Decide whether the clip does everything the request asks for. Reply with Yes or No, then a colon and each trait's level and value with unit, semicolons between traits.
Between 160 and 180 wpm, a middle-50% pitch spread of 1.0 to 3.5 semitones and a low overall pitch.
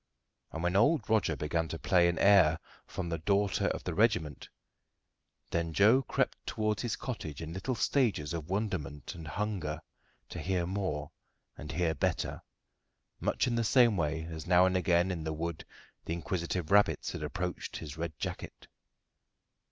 No: average, 165 wpm; average, 4.1 semitones; very low, 85 Hz